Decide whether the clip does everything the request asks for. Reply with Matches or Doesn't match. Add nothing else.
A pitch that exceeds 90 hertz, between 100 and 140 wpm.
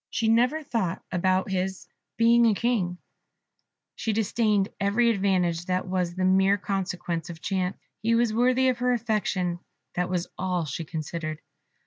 Doesn't match